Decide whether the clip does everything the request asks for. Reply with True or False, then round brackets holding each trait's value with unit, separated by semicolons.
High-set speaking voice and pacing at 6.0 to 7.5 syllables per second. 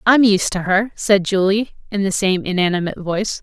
False (195 Hz; 5.4 syllables/s)